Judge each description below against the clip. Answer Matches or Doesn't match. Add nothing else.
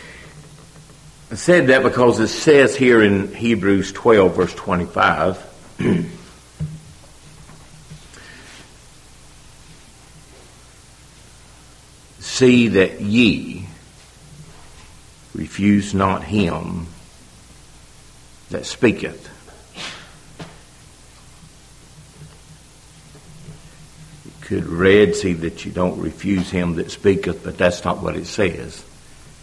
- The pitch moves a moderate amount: Doesn't match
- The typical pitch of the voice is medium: Doesn't match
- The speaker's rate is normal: Doesn't match